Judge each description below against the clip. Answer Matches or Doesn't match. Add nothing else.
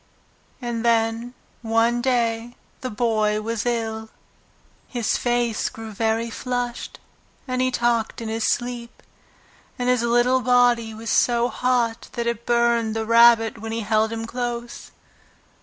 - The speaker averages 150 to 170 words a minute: Doesn't match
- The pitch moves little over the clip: Matches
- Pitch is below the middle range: Doesn't match